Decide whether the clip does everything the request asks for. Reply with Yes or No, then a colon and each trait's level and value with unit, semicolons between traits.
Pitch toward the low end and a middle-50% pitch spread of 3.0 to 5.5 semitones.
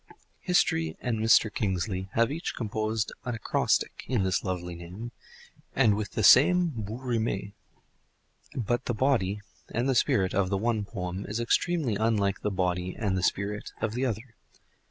Yes: low, 110 Hz; average, 3.8 semitones